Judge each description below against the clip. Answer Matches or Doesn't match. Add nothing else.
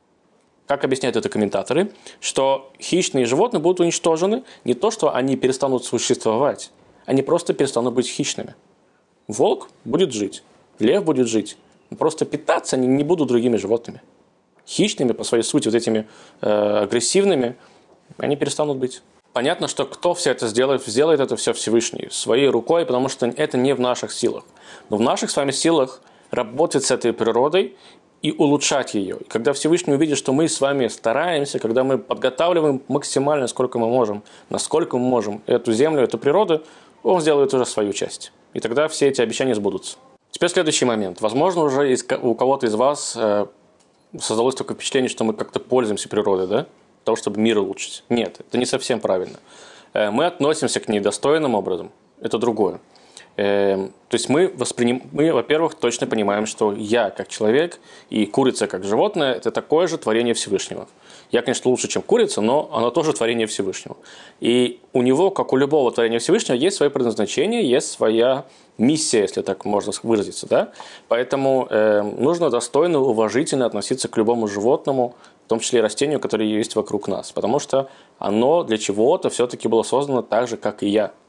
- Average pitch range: Matches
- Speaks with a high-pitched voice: Doesn't match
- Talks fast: Matches